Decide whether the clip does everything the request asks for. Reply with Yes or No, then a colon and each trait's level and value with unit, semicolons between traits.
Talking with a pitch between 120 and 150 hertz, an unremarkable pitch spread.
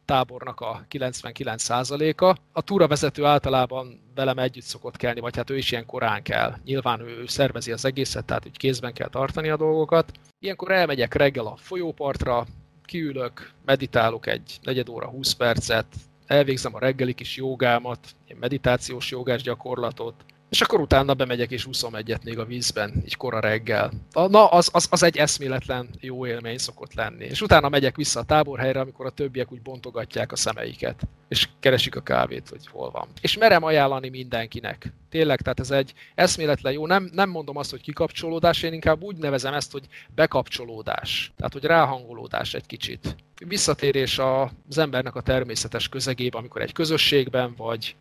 Yes: low, 130 Hz; average, 3.5 semitones